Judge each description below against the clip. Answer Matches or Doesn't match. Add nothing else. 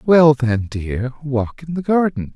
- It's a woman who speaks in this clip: Doesn't match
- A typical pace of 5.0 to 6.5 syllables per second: Doesn't match